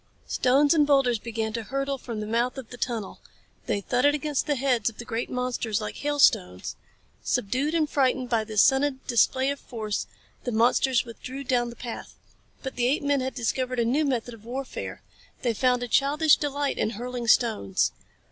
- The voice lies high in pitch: Yes, very high, 250 Hz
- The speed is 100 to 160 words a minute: No, average, 185 wpm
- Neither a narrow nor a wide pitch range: Yes, average, 3.0 semitones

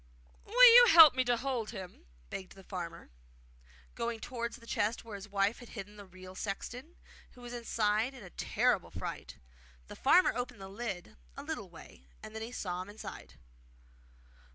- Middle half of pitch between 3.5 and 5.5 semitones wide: Yes, average, 4.2 semitones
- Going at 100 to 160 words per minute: No, average, 175 wpm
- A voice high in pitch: Yes, high, 220 Hz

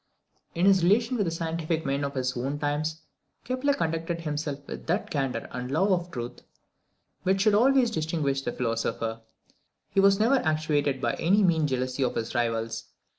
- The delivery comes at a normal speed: Yes, average, 175 wpm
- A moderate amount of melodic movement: No, wide, 5.9 semitones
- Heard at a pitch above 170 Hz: No, medium, 155 Hz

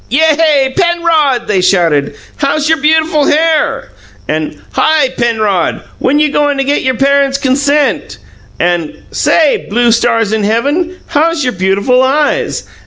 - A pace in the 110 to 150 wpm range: Yes, slow, 135 wpm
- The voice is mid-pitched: No, very high, 275 Hz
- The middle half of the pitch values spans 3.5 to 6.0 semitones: Yes, wide, 5.5 semitones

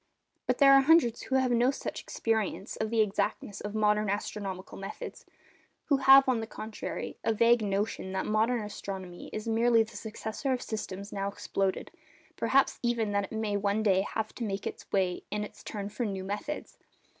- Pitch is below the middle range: No, high, 215 Hz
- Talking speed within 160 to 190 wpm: Yes, average, 180 wpm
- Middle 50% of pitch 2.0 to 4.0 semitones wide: Yes, average, 2.8 semitones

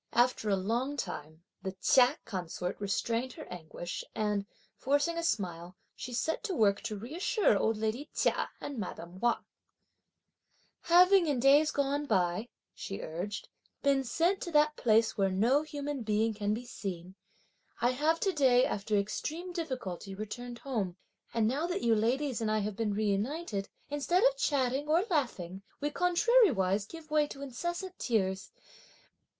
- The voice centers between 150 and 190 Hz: No, high, 240 Hz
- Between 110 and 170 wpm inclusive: Yes, average, 155 wpm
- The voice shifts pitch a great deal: Yes, wide, 6.6 semitones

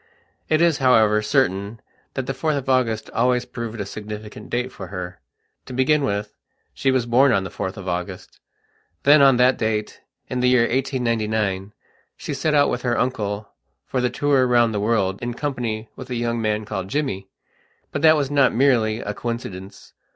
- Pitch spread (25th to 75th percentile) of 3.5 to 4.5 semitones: Yes, average, 3.8 semitones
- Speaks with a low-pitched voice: Yes, low, 120 Hz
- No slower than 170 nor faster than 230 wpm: Yes, average, 185 wpm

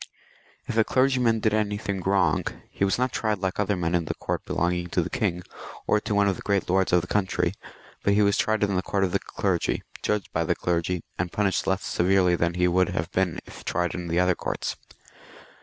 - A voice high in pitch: No, very low, 95 Hz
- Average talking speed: No, fast, 230 wpm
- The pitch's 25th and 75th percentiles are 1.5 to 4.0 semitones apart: Yes, narrow, 2.6 semitones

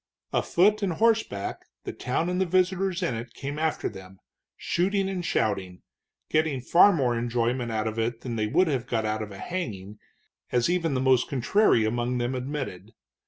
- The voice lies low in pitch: Yes, low, 125 Hz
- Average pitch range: No, wide, 7.5 semitones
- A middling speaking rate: Yes, average, 180 wpm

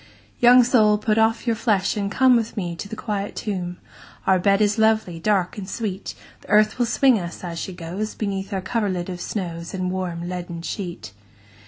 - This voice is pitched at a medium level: No, high, 200 Hz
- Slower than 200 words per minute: No, fast, 205 wpm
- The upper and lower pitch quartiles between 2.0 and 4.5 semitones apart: Yes, average, 3.4 semitones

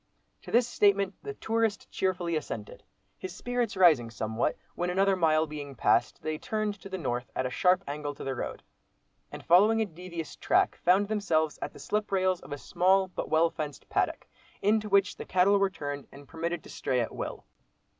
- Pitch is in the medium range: Yes, medium, 180 Hz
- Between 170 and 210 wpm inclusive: Yes, average, 195 wpm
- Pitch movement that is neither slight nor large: Yes, average, 4.8 semitones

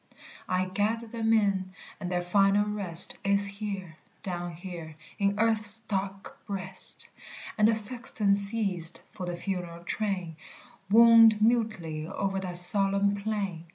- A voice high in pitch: Yes, high, 200 Hz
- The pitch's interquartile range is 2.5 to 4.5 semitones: Yes, average, 2.8 semitones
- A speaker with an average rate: No, slow, 130 wpm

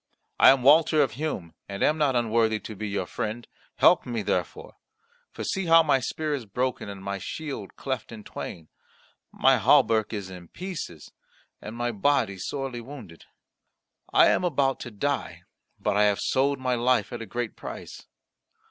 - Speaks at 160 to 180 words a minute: Yes, average, 175 wpm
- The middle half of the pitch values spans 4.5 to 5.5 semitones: Yes, average, 5.2 semitones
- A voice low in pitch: Yes, low, 120 Hz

